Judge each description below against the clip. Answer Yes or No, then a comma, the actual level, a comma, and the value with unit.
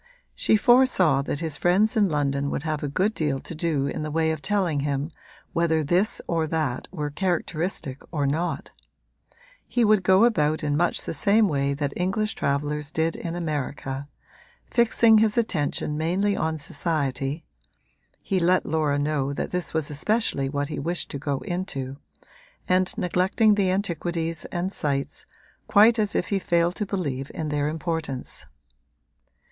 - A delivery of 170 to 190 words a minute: No, average, 160 wpm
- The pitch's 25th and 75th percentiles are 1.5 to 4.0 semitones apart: No, average, 4.5 semitones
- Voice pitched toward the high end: No, medium, 160 Hz